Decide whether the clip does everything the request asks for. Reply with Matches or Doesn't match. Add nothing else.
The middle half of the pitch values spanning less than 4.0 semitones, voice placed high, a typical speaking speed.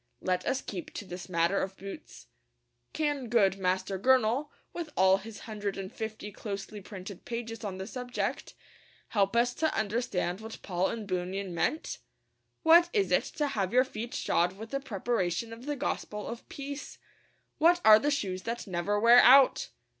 Doesn't match